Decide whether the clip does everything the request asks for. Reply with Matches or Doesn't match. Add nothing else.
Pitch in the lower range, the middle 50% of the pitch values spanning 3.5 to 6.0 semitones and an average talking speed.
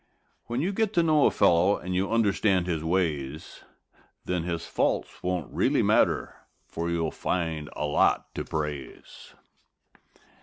Matches